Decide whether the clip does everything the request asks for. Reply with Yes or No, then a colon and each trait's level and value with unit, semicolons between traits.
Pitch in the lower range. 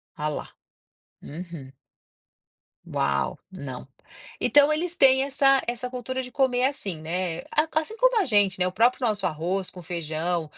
No: high, 205 Hz